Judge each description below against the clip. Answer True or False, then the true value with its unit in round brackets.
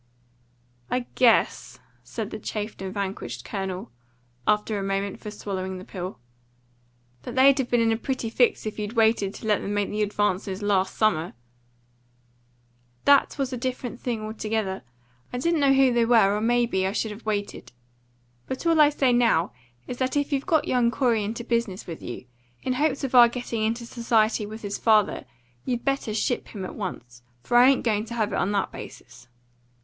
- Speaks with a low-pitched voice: False (220 Hz)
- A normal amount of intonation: True (3.5 semitones)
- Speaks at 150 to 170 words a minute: False (190 wpm)